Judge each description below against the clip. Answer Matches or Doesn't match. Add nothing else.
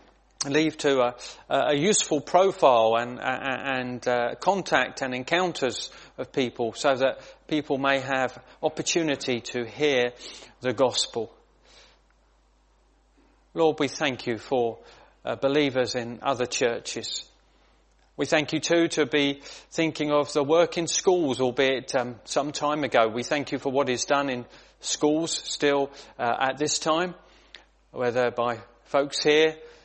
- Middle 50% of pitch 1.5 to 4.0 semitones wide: Matches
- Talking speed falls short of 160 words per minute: Matches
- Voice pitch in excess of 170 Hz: Doesn't match